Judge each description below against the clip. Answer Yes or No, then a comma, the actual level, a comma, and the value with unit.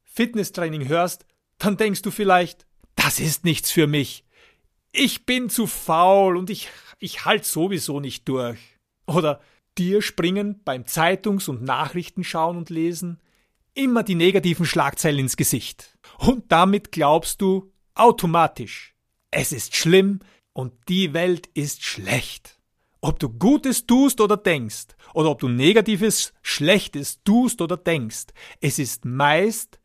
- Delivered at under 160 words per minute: Yes, average, 135 wpm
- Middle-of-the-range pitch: Yes, medium, 175 Hz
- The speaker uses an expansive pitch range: Yes, wide, 5.7 semitones